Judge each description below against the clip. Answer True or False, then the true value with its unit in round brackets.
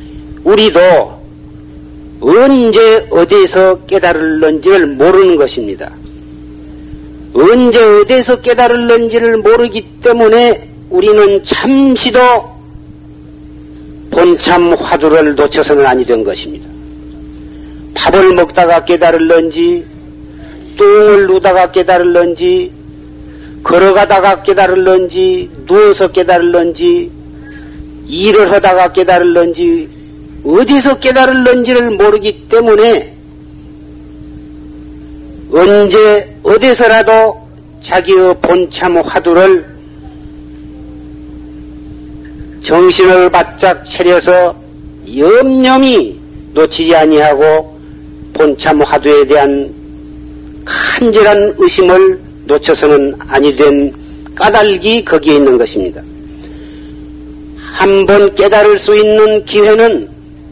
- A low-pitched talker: False (170 Hz)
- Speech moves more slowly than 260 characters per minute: True (200 characters per minute)